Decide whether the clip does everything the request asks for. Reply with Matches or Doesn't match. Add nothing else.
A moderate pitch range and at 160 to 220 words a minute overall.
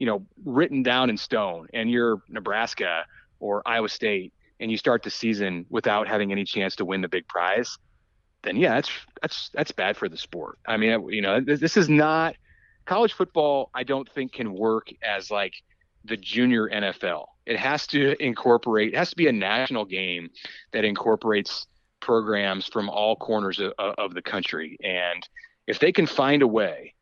Matches